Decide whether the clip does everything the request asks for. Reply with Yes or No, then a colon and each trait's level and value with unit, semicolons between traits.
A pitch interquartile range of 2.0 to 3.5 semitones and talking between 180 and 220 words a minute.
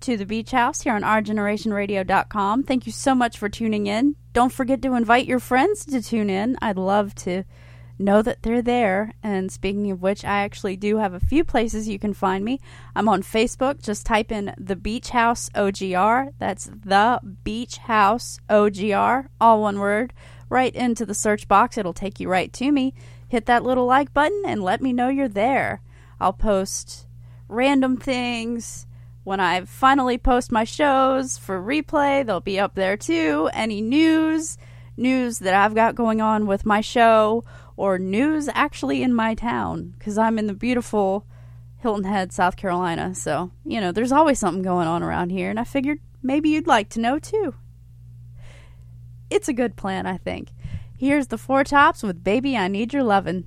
No: average, 4.8 semitones; average, 185 wpm